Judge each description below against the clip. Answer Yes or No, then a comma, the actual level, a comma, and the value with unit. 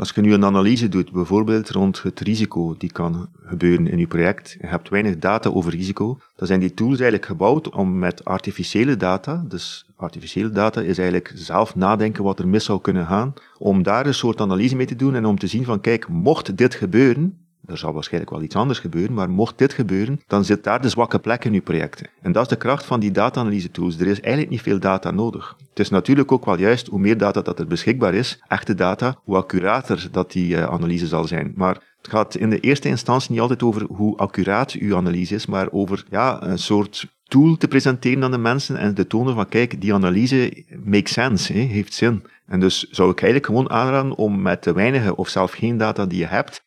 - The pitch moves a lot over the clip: No, average, 4.7 semitones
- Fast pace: Yes, fast, 230 wpm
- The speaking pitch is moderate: No, low, 105 Hz